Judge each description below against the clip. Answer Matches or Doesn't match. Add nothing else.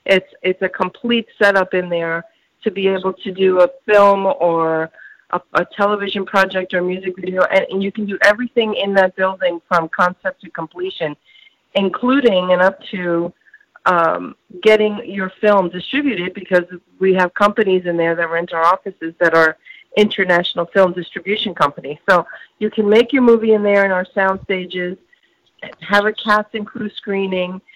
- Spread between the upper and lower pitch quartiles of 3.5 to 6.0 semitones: Doesn't match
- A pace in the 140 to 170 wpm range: Matches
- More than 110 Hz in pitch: Matches